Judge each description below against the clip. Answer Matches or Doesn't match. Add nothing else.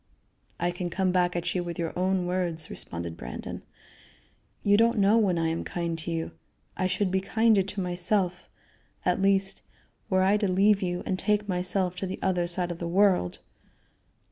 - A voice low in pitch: Doesn't match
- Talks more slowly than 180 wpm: Doesn't match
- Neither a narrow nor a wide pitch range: Doesn't match